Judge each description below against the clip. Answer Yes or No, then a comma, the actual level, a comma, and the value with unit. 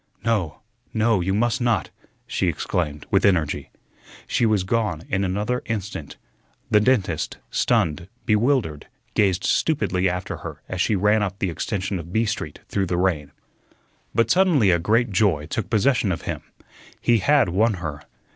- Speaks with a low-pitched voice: Yes, low, 100 Hz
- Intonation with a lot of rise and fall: No, average, 4.2 semitones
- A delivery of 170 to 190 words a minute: No, average, 155 wpm